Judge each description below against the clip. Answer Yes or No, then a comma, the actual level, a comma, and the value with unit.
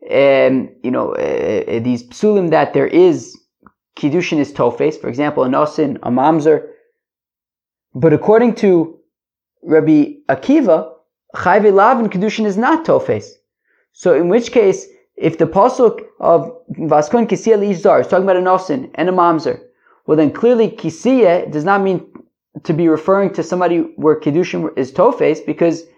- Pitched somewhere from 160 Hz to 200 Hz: Yes, high, 190 Hz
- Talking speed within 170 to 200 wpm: No, average, 160 wpm